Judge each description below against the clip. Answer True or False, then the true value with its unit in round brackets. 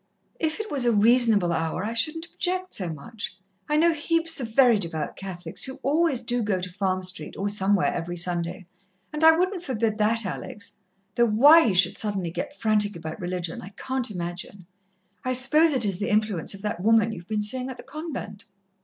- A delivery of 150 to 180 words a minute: False (200 wpm)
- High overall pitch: True (215 Hz)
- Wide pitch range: True (6.1 semitones)